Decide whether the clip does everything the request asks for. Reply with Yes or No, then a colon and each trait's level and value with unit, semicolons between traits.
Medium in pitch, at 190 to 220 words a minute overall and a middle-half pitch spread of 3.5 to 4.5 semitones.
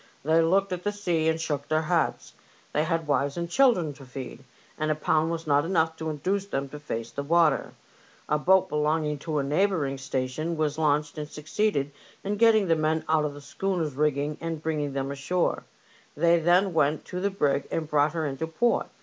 No: medium, 155 Hz; fast, 205 wpm; average, 2.8 semitones